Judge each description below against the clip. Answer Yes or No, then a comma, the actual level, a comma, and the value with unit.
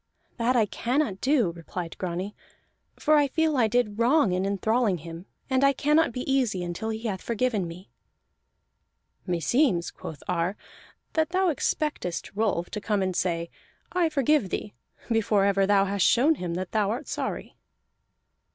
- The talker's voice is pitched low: No, high, 215 Hz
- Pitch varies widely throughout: Yes, wide, 6.3 semitones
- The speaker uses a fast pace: No, average, 160 wpm